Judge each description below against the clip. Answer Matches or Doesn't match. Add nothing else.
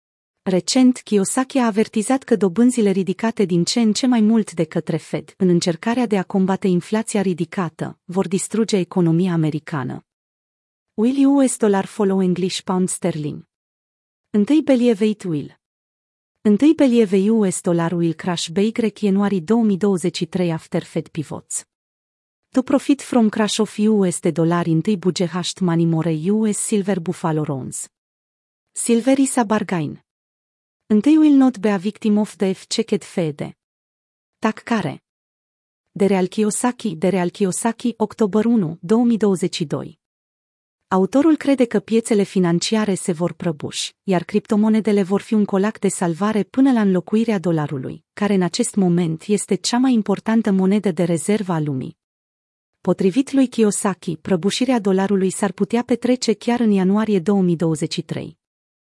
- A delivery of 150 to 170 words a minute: Doesn't match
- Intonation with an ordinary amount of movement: Matches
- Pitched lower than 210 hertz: Matches